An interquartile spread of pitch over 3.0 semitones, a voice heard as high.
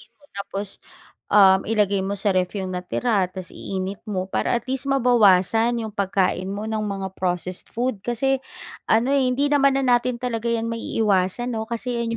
Yes: average, 4.1 semitones; high, 220 Hz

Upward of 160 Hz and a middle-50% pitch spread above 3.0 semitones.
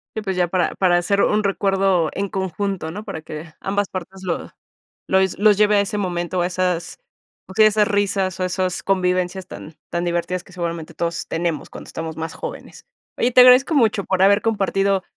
No: high, 190 Hz; narrow, 2.4 semitones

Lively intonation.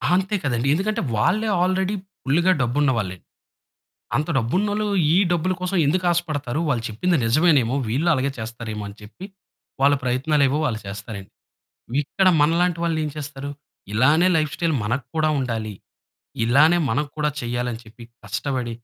Yes: wide, 6.4 semitones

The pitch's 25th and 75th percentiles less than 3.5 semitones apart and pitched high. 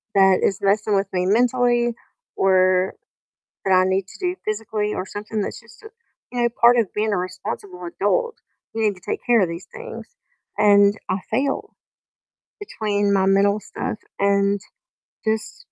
Yes: average, 3.0 semitones; high, 205 Hz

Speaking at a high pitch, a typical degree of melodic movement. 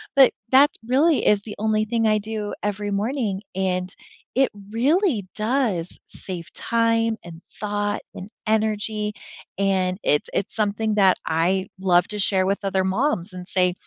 Yes: high, 205 Hz; average, 3.0 semitones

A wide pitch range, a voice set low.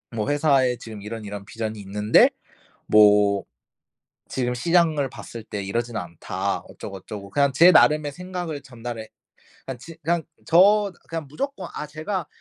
Yes: wide, 7.1 semitones; low, 130 Hz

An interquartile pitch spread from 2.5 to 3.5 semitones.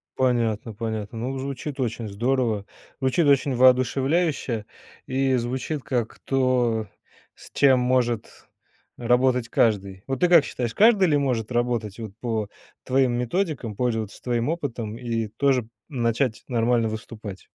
Yes: average, 2.9 semitones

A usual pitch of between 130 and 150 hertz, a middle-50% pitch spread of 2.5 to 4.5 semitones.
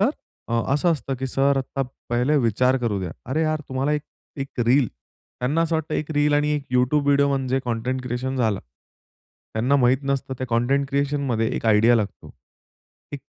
Yes: low, 135 Hz; average, 2.8 semitones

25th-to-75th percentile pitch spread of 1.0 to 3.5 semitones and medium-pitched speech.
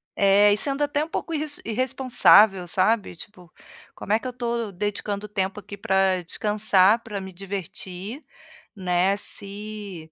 No: average, 2.9 semitones; high, 205 Hz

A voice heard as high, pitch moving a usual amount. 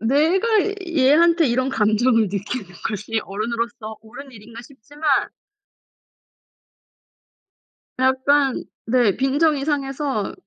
Yes: very high, 260 Hz; average, 4.3 semitones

